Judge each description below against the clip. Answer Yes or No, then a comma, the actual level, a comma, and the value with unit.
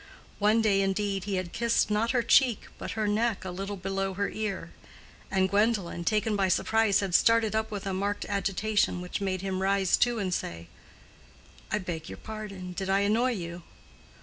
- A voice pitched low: No, high, 200 Hz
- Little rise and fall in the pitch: Yes, narrow, 2.3 semitones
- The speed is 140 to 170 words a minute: No, average, 180 wpm